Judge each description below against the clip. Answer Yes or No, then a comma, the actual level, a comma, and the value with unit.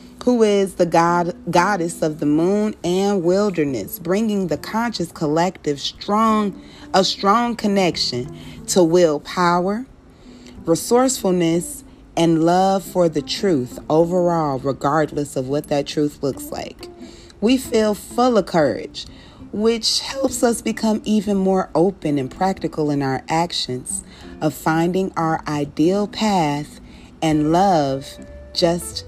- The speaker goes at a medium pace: No, slow, 120 wpm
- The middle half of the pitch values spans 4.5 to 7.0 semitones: Yes, average, 5.0 semitones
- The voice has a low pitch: No, medium, 175 Hz